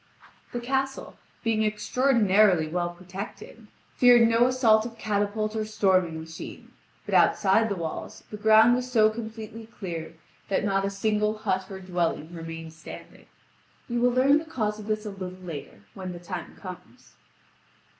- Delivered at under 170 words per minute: Yes, average, 155 wpm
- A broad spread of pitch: No, average, 3.7 semitones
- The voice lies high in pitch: Yes, high, 210 Hz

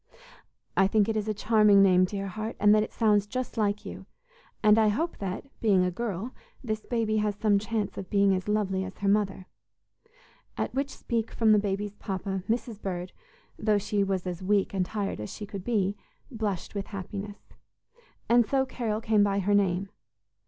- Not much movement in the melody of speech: Yes, narrow, 2.0 semitones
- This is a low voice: No, high, 205 Hz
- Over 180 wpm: Yes, average, 190 wpm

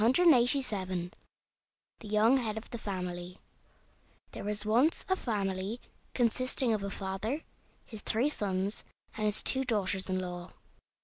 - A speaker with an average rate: No, slow, 130 wpm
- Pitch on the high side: Yes, high, 210 Hz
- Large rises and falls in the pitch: No, average, 4.2 semitones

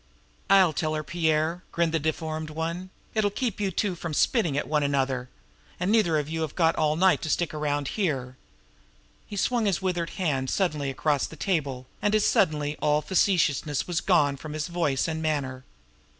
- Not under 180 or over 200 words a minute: Yes, average, 190 wpm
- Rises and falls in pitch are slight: No, average, 3.5 semitones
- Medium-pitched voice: Yes, medium, 160 Hz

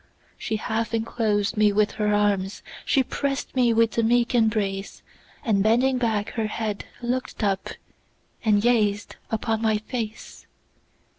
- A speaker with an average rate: No, slow, 125 wpm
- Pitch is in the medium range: No, high, 220 Hz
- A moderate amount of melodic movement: No, narrow, 2.1 semitones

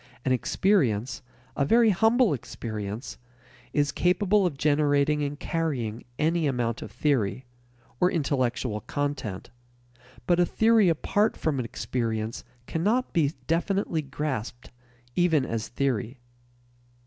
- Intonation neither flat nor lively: No, wide, 6.1 semitones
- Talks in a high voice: No, medium, 145 Hz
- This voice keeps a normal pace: No, slow, 115 wpm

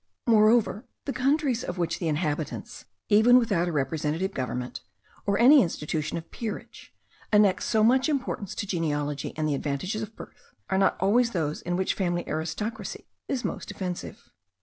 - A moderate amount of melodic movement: No, wide, 6.1 semitones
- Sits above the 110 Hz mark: Yes, high, 190 Hz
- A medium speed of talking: Yes, average, 160 wpm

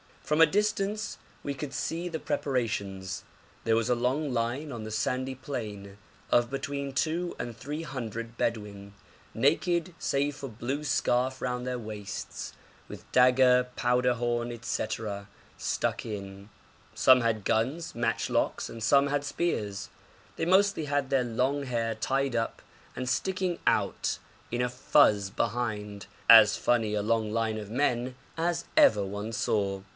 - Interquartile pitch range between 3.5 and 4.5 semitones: Yes, average, 4.2 semitones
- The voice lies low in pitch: Yes, low, 125 Hz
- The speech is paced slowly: No, average, 150 wpm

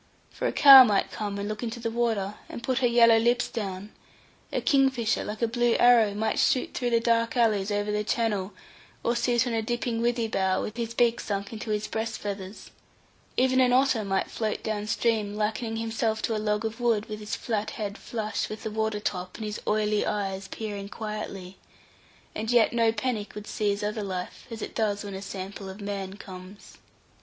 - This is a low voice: No, high, 215 Hz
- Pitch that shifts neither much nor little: No, narrow, 2.3 semitones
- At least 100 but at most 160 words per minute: No, average, 200 wpm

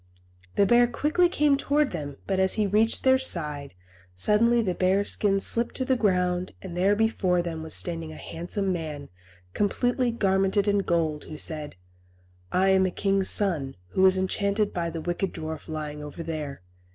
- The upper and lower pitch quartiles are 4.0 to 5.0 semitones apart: Yes, average, 4.4 semitones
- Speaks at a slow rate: No, average, 175 wpm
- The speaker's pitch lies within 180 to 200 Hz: Yes, high, 190 Hz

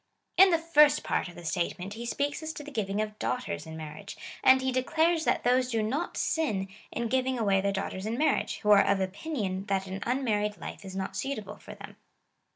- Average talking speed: No, fast, 210 wpm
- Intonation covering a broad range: Yes, wide, 5.9 semitones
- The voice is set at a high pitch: Yes, high, 215 Hz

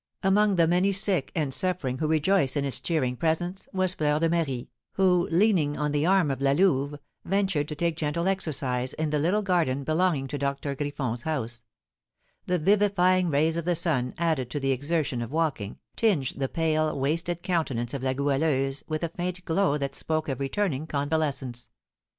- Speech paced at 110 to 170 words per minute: No, average, 180 wpm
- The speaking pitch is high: No, medium, 155 Hz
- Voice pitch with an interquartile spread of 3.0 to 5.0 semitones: Yes, average, 4.3 semitones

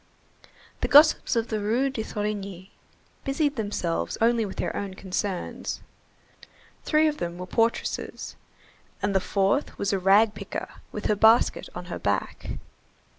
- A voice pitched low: No, high, 210 Hz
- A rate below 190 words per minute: Yes, average, 145 wpm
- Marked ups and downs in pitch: No, average, 3.1 semitones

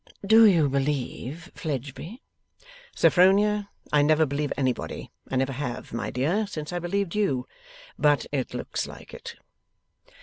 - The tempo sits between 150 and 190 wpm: No, slow, 135 wpm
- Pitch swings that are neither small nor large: No, wide, 6.1 semitones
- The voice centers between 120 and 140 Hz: No, medium, 150 Hz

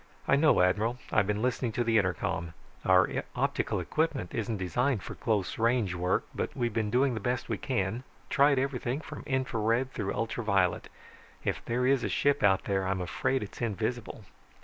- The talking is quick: No, average, 185 wpm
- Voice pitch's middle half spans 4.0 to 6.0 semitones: Yes, average, 4.4 semitones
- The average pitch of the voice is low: Yes, low, 115 Hz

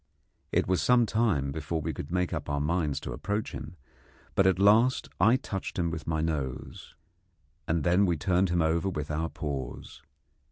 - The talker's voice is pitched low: Yes, very low, 85 Hz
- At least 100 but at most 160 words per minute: No, average, 185 wpm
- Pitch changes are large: No, average, 4.1 semitones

